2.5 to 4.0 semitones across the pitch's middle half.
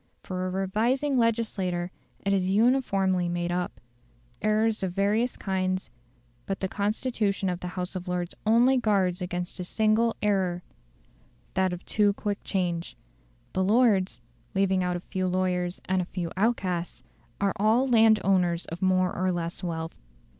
Yes: average, 2.9 semitones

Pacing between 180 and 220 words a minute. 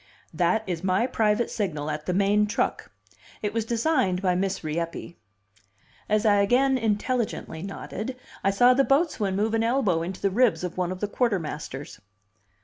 No: average, 165 wpm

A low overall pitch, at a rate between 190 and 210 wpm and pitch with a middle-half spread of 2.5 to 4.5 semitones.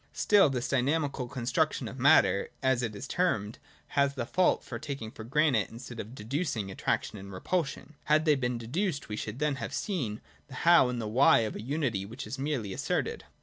No: low, 125 Hz; average, 195 wpm; average, 5.1 semitones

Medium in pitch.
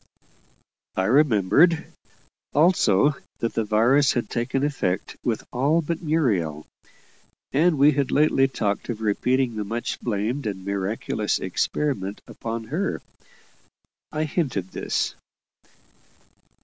No: low, 120 Hz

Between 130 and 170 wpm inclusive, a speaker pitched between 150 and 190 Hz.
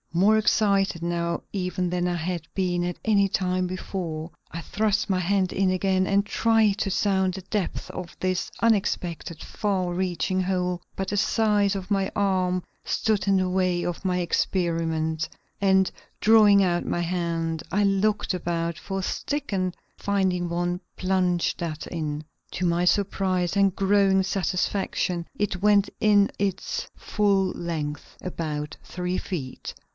Yes: average, 150 wpm; medium, 185 Hz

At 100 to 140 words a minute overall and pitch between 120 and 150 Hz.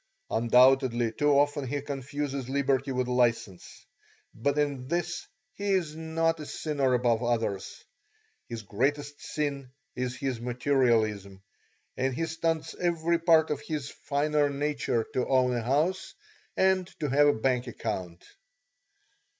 Yes: slow, 135 wpm; low, 135 Hz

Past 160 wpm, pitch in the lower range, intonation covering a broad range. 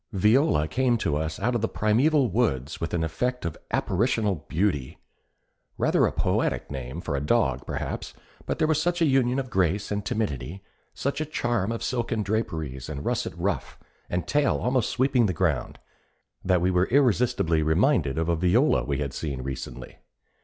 Yes: average, 175 wpm; low, 100 Hz; wide, 7.9 semitones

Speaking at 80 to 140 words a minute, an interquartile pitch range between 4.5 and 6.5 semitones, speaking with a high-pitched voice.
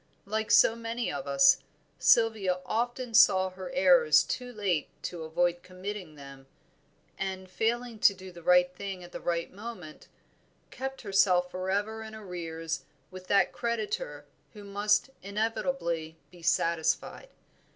No: slow, 135 wpm; average, 4.0 semitones; high, 195 Hz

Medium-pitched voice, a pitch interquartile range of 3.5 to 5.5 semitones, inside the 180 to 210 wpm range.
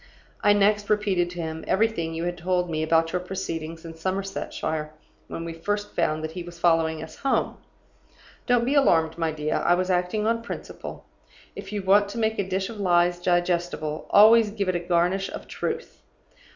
Yes: medium, 180 Hz; average, 3.8 semitones; average, 190 wpm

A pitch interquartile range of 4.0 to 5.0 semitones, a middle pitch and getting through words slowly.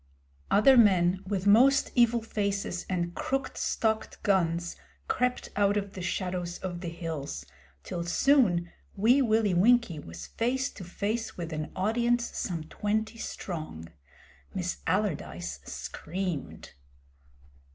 No: average, 4.6 semitones; high, 195 Hz; slow, 120 wpm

